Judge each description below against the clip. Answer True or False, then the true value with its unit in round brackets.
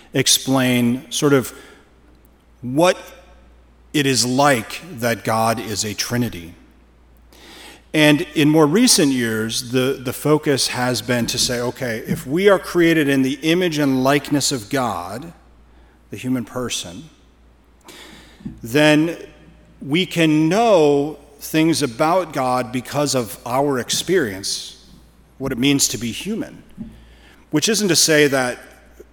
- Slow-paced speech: True (125 wpm)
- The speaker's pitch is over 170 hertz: False (130 Hz)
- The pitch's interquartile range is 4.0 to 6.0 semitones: True (4.6 semitones)